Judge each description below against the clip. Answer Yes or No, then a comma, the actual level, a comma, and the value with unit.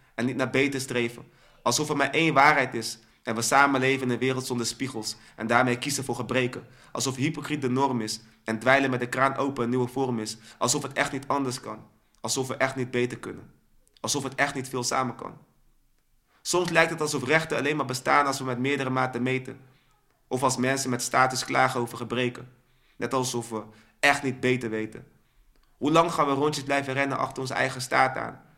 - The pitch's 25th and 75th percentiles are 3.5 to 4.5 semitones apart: No, narrow, 2.5 semitones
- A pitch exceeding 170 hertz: No, low, 130 Hz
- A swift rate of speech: Yes, fast, 210 wpm